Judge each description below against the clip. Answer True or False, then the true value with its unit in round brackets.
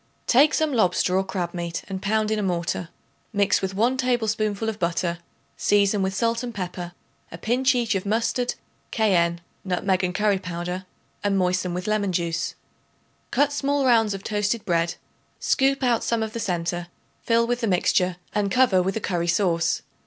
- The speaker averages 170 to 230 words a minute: True (175 wpm)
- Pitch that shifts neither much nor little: True (4.2 semitones)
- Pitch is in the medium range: False (200 Hz)